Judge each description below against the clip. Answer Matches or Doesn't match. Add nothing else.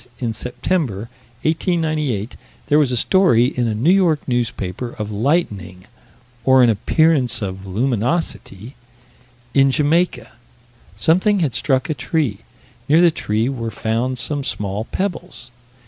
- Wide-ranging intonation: Matches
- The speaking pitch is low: Matches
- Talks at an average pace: Doesn't match